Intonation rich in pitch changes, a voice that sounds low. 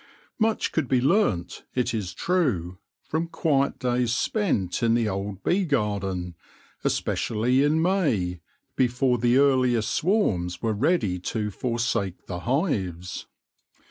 Yes: wide, 6.9 semitones; low, 120 Hz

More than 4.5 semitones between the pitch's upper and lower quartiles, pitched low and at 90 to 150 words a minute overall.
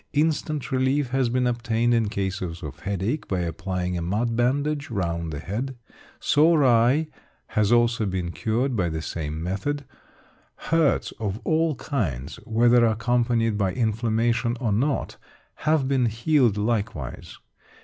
Yes: average, 5.1 semitones; low, 115 Hz; average, 140 wpm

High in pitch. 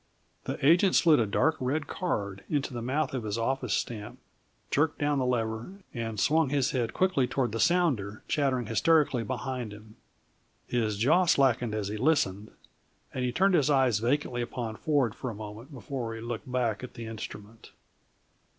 No: low, 125 Hz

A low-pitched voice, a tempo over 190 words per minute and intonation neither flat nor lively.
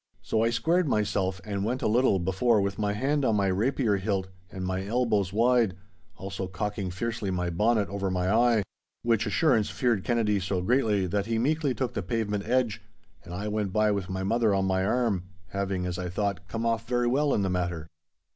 Yes: low, 105 Hz; average, 200 wpm; average, 3.6 semitones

